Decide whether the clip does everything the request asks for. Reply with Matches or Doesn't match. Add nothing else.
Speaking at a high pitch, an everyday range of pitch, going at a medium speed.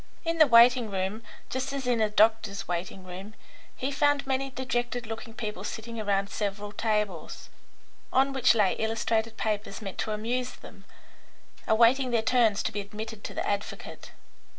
Matches